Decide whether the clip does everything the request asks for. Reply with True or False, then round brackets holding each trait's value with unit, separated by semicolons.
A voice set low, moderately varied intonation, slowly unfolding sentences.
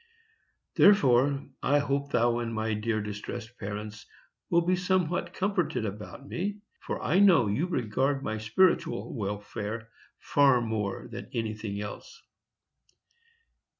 False (120 Hz; 6.7 semitones; 120 wpm)